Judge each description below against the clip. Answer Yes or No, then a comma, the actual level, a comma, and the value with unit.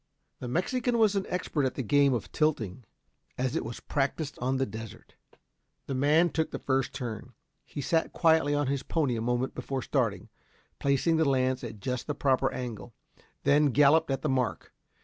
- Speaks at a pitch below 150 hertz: Yes, low, 135 Hz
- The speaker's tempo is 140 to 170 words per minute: No, average, 185 wpm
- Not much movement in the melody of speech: No, average, 3.4 semitones